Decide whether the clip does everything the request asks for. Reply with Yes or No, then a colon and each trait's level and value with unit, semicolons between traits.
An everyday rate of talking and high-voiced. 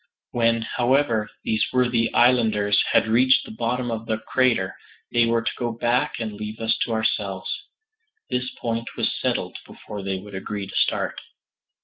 No: average, 160 wpm; low, 115 Hz